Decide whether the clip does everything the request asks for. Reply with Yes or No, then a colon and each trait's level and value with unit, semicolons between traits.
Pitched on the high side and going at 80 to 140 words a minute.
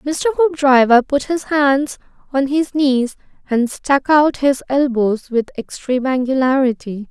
Yes: very high, 270 Hz; slow, 135 wpm